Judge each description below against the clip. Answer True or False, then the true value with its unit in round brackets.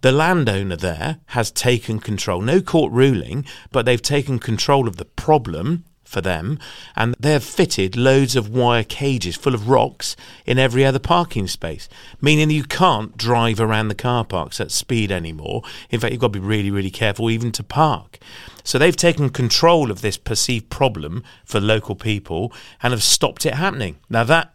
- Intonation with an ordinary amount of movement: True (4.6 semitones)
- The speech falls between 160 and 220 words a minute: True (180 wpm)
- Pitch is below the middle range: True (120 Hz)